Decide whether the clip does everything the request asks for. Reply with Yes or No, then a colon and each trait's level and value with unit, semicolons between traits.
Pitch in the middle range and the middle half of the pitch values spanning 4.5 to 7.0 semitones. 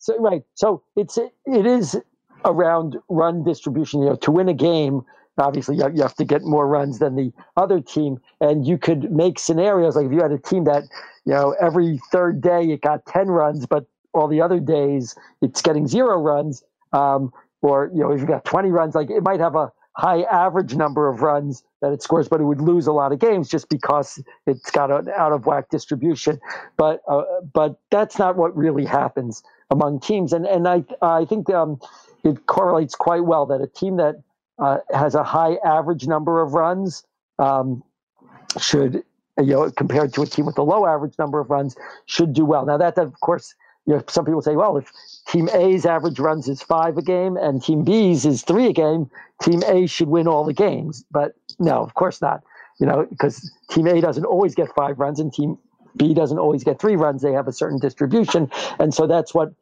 No: medium, 155 Hz; average, 3.0 semitones